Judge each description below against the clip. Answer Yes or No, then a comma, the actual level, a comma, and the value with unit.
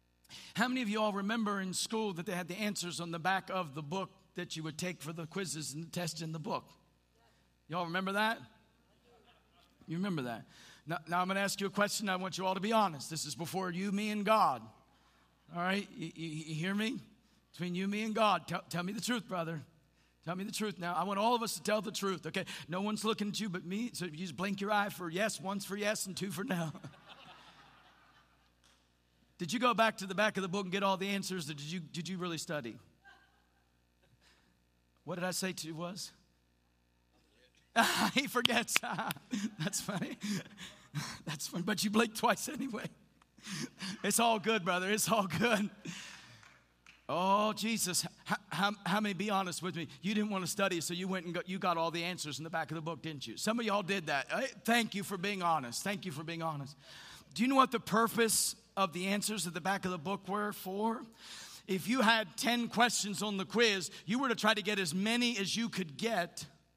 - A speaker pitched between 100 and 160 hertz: No, high, 190 Hz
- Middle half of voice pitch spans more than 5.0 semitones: No, average, 4.0 semitones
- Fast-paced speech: Yes, fast, 220 wpm